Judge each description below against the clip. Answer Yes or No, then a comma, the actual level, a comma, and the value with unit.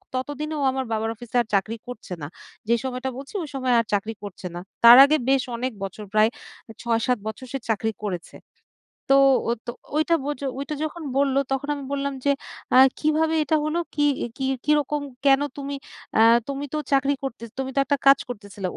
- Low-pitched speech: No, very high, 265 Hz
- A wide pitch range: No, average, 3.9 semitones